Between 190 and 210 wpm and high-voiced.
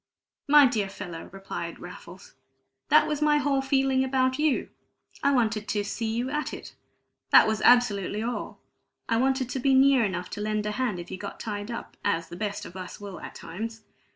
Yes: average, 195 wpm; high, 225 Hz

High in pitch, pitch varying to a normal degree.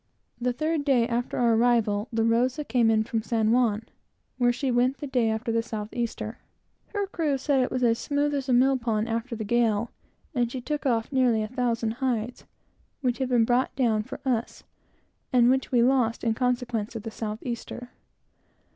No: high, 240 Hz; narrow, 2.2 semitones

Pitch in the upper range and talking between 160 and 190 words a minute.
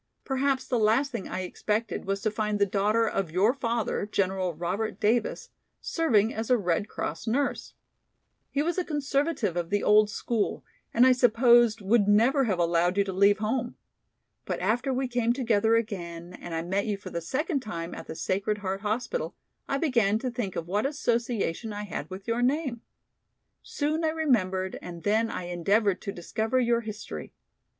Yes: high, 215 Hz; average, 180 wpm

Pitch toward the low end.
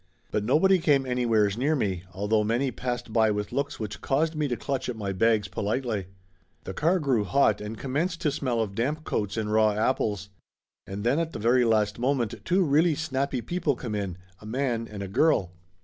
Yes: low, 120 Hz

